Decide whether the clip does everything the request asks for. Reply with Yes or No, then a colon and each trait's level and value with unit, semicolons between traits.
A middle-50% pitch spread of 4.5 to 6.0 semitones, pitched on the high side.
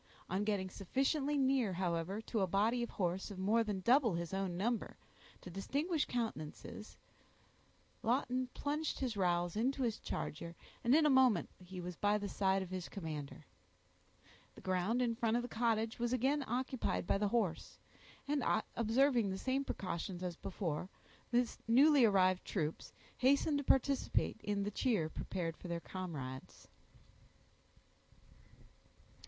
Yes: wide, 5.5 semitones; high, 210 Hz